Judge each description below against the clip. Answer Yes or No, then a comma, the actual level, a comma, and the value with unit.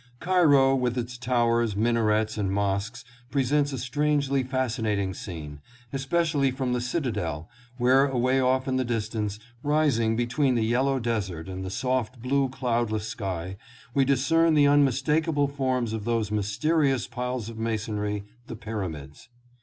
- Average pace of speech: Yes, average, 145 wpm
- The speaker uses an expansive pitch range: No, average, 4.0 semitones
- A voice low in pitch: Yes, low, 125 Hz